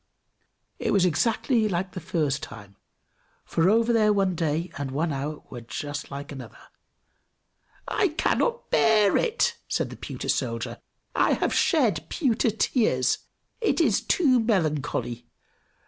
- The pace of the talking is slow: Yes, slow, 130 wpm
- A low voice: No, medium, 185 Hz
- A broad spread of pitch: Yes, wide, 7.9 semitones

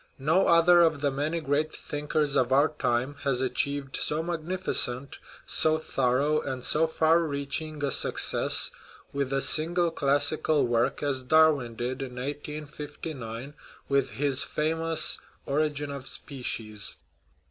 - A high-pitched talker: No, medium, 145 Hz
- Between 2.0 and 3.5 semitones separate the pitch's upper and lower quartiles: Yes, average, 2.7 semitones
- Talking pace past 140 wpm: No, slow, 135 wpm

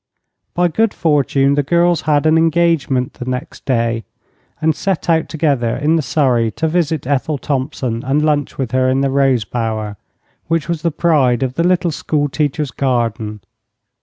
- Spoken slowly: No, average, 170 wpm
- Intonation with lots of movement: No, average, 4.1 semitones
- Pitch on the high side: No, medium, 145 Hz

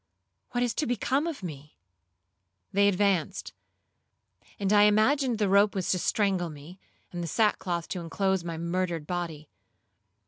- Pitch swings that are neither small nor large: Yes, average, 3.5 semitones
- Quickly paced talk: No, average, 145 wpm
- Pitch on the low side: No, high, 190 Hz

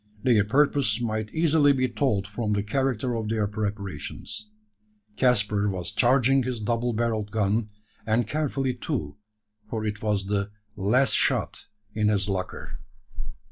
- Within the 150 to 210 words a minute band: No, average, 140 wpm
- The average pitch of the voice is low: Yes, low, 110 Hz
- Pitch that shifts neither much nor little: Yes, average, 3.5 semitones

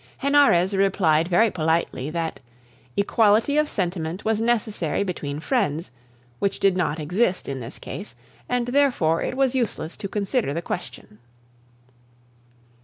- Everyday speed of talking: No, slow, 130 wpm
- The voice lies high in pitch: Yes, high, 195 Hz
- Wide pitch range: Yes, wide, 6.0 semitones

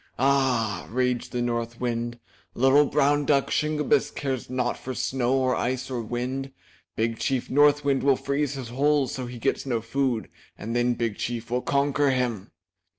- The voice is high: No, low, 130 Hz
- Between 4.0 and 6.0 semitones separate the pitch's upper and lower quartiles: No, narrow, 2.6 semitones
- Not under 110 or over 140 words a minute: No, average, 170 wpm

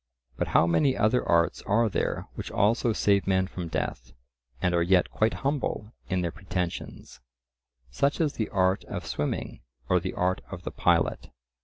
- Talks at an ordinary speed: Yes, average, 165 wpm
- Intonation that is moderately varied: Yes, average, 4.1 semitones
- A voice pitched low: Yes, very low, 95 Hz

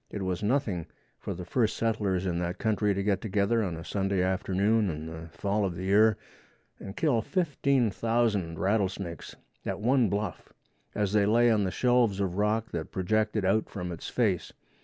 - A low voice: Yes, low, 100 Hz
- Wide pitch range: No, average, 3.1 semitones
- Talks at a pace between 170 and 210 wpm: Yes, average, 180 wpm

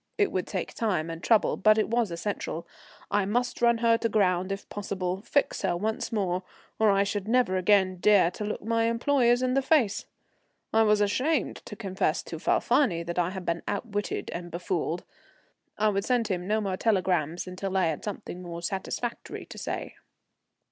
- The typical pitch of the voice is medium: No, high, 200 Hz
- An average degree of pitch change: Yes, average, 3.8 semitones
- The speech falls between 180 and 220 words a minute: Yes, average, 185 wpm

